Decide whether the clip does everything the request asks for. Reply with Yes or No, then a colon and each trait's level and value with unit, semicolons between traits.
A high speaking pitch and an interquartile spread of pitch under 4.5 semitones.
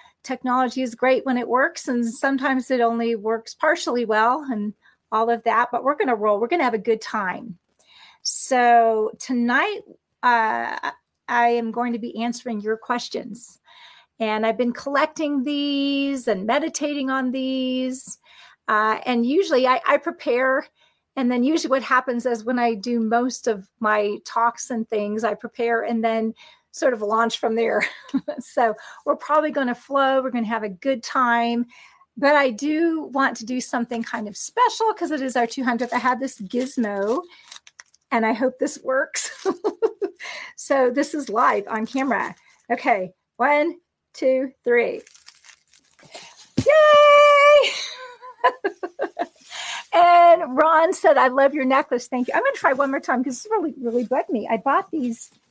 Yes: very high, 255 Hz; average, 3.8 semitones